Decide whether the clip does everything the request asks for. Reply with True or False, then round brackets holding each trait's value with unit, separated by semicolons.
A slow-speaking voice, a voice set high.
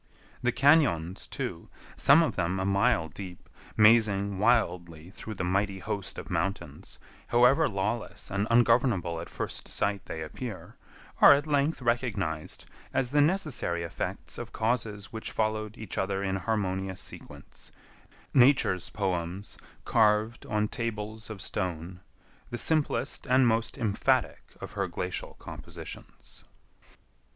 False (125 wpm; 105 Hz)